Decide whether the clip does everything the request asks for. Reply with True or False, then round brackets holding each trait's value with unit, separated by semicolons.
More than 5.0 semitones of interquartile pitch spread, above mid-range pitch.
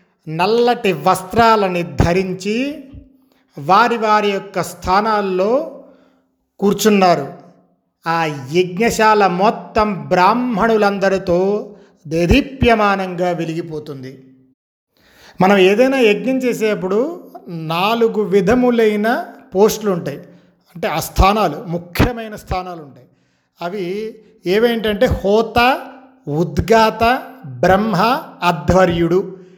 False (4.3 semitones; 195 Hz)